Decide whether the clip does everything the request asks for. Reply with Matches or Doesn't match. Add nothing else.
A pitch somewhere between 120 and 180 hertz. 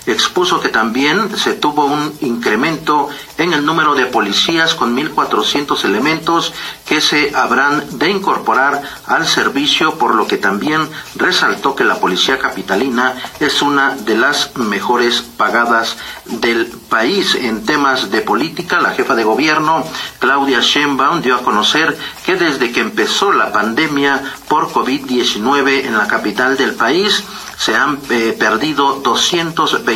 Matches